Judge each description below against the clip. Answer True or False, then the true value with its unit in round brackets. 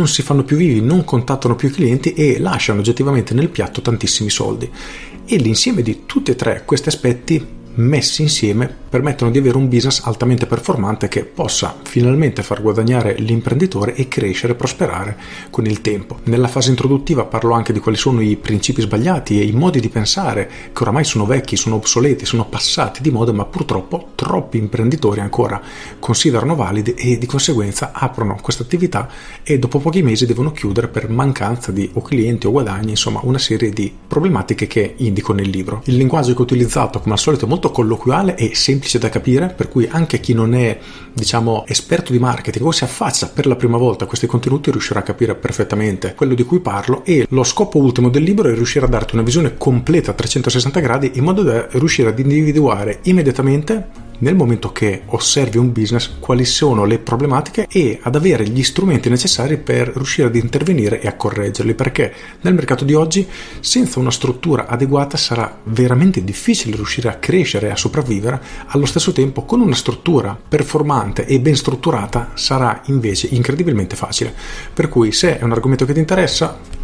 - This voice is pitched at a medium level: False (125 Hz)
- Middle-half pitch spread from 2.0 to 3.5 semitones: False (4.0 semitones)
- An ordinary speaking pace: False (185 wpm)